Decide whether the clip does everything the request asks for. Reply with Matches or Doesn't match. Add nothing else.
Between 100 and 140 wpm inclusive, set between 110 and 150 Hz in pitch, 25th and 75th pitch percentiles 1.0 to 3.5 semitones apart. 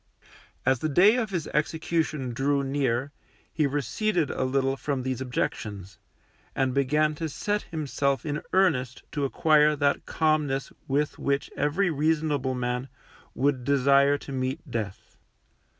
Matches